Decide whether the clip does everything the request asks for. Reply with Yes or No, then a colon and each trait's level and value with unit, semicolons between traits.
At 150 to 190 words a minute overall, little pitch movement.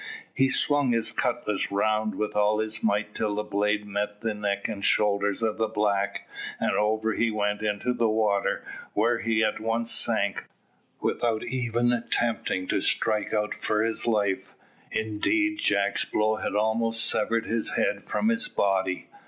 Yes: average, 160 wpm; narrow, 1.8 semitones